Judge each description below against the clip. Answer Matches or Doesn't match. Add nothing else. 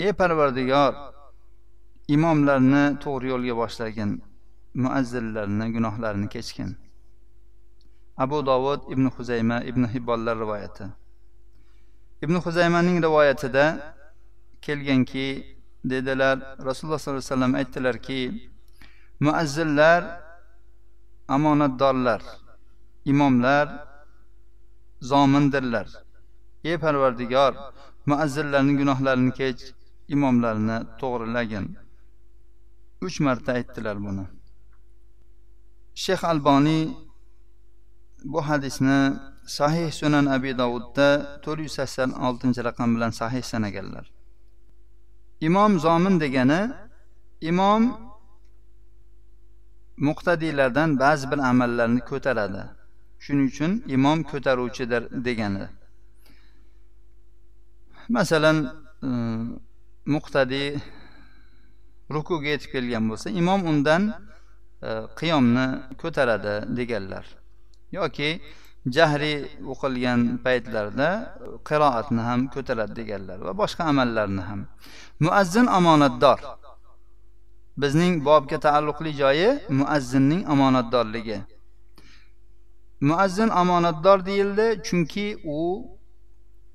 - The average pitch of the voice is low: Matches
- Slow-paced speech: Matches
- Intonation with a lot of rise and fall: Doesn't match